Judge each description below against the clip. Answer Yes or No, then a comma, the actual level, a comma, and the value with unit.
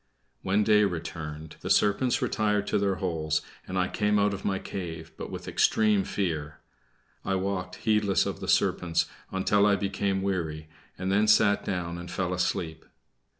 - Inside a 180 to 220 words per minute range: No, average, 165 wpm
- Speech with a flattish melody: No, average, 3.0 semitones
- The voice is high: No, very low, 95 Hz